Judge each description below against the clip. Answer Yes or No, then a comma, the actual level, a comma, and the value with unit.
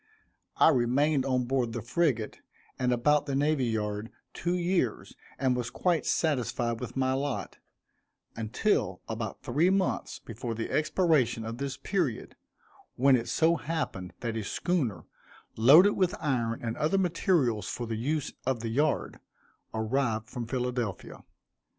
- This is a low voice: Yes, low, 130 Hz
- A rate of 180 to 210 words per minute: No, average, 145 wpm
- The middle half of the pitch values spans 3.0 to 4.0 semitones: No, average, 5.0 semitones